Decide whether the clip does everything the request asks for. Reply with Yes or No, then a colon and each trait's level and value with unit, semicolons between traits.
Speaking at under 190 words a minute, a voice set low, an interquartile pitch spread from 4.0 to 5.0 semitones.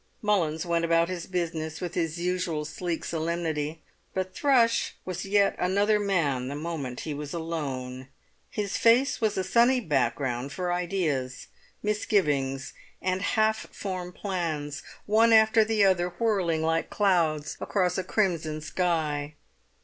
No: slow, 135 wpm; medium, 175 Hz; average, 4.3 semitones